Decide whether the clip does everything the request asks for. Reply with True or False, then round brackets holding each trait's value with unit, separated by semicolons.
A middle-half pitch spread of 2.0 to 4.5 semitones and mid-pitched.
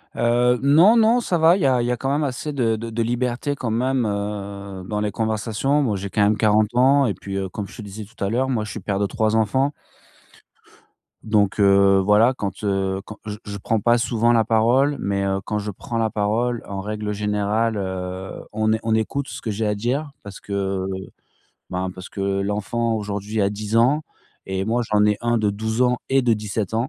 False (2.9 semitones; 110 Hz)